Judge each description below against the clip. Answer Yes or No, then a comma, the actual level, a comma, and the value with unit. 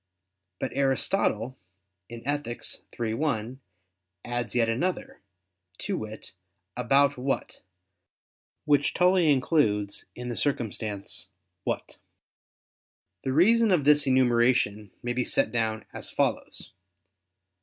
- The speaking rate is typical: No, slow, 105 wpm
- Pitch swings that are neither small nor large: Yes, average, 4.1 semitones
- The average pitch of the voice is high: No, low, 125 Hz